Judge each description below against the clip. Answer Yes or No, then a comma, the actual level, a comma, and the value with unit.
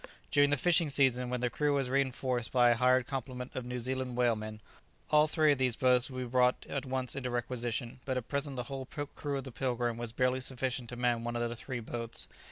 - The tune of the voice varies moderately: No, narrow, 1.9 semitones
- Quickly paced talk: Yes, fast, 230 wpm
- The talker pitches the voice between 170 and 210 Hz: No, low, 125 Hz